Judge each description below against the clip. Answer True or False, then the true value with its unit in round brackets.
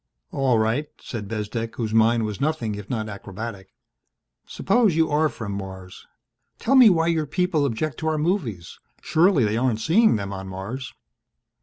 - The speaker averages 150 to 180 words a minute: True (165 wpm)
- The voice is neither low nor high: False (120 Hz)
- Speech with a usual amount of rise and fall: False (7.0 semitones)